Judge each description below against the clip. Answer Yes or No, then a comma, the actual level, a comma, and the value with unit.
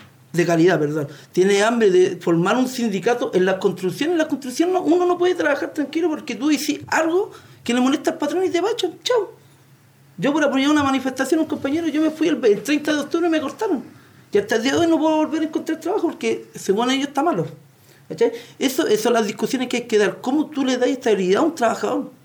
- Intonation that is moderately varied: No, wide, 7.6 semitones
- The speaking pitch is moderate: No, very high, 270 Hz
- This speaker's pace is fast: Yes, fast, 230 wpm